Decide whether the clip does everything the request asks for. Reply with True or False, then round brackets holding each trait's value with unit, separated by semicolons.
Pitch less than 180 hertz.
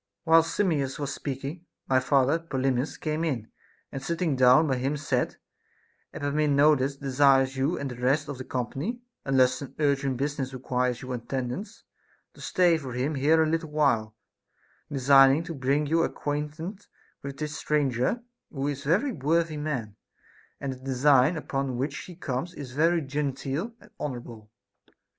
True (140 Hz)